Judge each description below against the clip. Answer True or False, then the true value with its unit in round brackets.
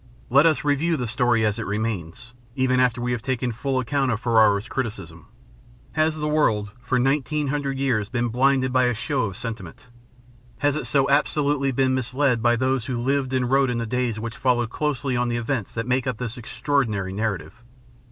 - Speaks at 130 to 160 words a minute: False (195 wpm)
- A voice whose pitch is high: False (125 Hz)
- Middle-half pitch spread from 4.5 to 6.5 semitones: False (3.0 semitones)